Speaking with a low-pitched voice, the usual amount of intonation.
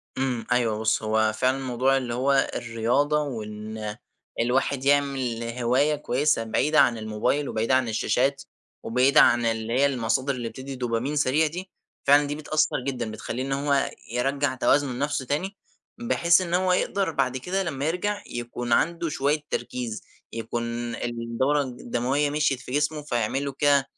Yes: low, 130 Hz; average, 3.6 semitones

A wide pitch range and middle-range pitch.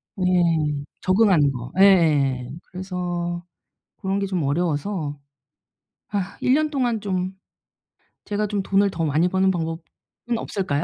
No: average, 3.9 semitones; medium, 180 Hz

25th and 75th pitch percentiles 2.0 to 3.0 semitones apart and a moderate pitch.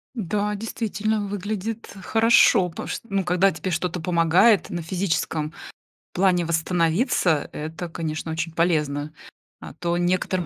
No: average, 3.5 semitones; medium, 180 Hz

